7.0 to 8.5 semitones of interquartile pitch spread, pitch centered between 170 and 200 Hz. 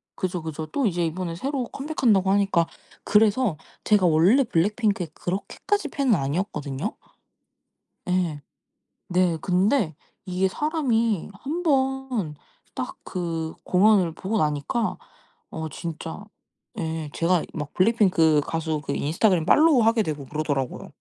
No: wide, 5.9 semitones; medium, 185 Hz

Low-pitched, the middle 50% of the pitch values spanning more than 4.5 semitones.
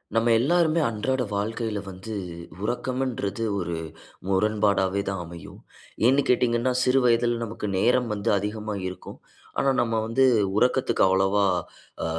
No: low, 115 Hz; average, 3.8 semitones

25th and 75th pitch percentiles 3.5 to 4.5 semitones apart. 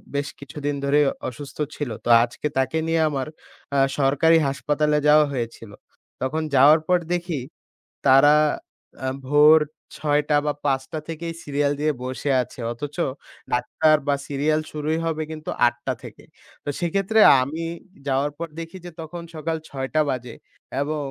No: narrow, 2.6 semitones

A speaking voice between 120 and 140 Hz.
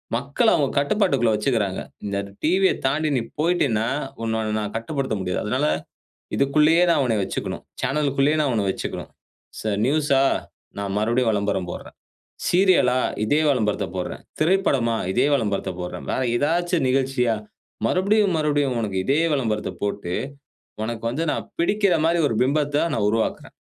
Yes: low, 135 Hz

